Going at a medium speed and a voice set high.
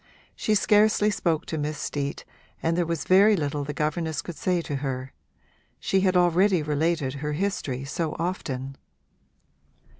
No: average, 150 wpm; medium, 160 Hz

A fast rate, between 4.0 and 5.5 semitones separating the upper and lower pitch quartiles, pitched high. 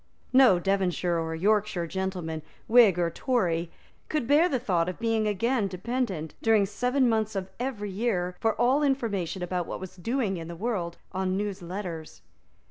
No: average, 160 wpm; average, 4.7 semitones; high, 195 Hz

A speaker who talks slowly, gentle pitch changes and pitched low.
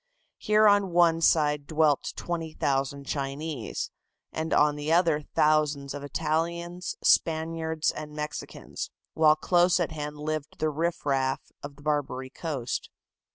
No: slow, 130 wpm; narrow, 2.3 semitones; medium, 155 Hz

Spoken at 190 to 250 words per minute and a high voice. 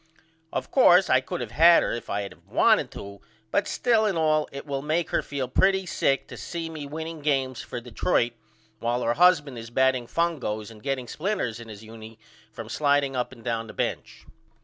No: fast, 205 wpm; low, 135 Hz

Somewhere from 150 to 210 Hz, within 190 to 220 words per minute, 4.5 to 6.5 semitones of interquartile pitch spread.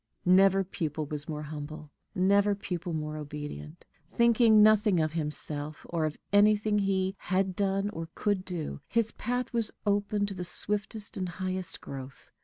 No: medium, 185 Hz; average, 155 wpm; average, 4.9 semitones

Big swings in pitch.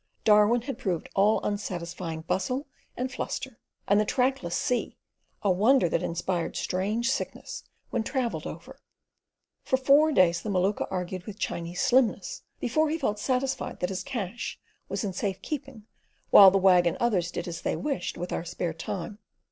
Yes: wide, 6.0 semitones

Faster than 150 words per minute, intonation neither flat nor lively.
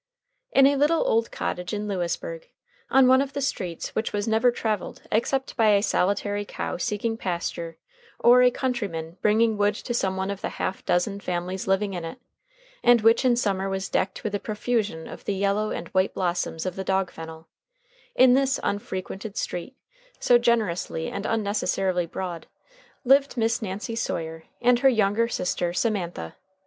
Yes: average, 170 wpm; average, 4.2 semitones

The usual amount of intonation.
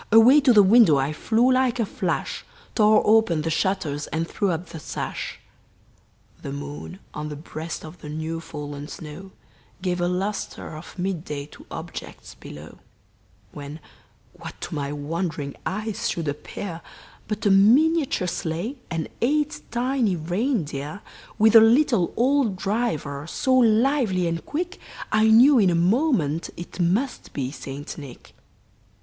No: wide, 6.8 semitones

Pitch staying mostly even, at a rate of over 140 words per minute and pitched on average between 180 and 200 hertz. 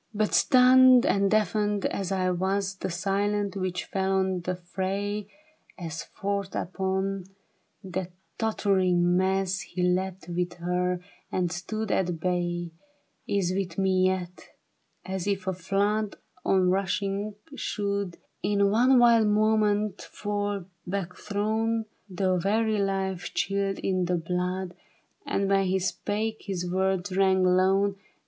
No: narrow, 2.0 semitones; slow, 135 wpm; high, 190 Hz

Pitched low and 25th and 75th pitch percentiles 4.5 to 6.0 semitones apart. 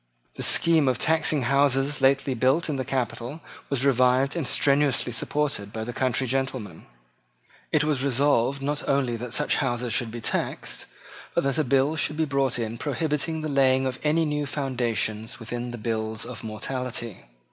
No: low, 130 Hz; average, 3.1 semitones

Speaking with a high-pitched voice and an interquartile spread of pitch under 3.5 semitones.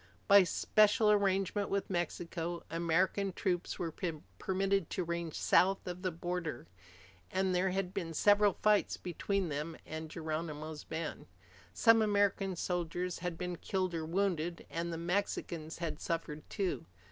No: medium, 175 Hz; average, 2.9 semitones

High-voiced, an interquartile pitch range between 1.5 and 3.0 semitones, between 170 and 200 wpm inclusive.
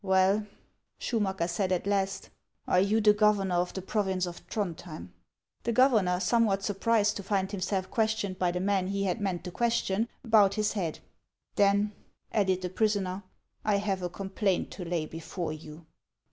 Yes: high, 195 Hz; narrow, 2.5 semitones; average, 190 wpm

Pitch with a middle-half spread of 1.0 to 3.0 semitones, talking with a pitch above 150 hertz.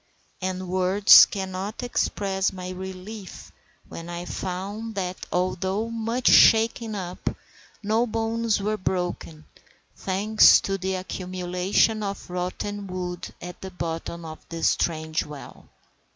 Yes: narrow, 2.5 semitones; high, 190 Hz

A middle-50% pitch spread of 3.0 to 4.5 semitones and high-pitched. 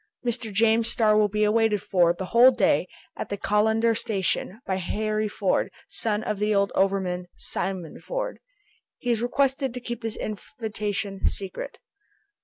No: narrow, 2.6 semitones; high, 215 Hz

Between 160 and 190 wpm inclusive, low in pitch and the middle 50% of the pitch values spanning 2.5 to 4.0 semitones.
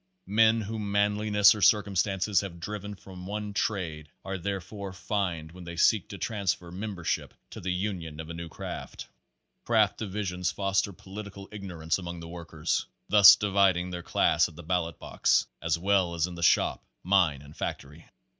Yes: average, 170 wpm; very low, 95 Hz; average, 3.0 semitones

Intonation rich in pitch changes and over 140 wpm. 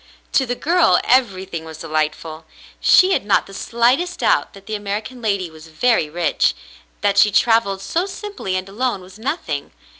Yes: wide, 5.9 semitones; average, 170 wpm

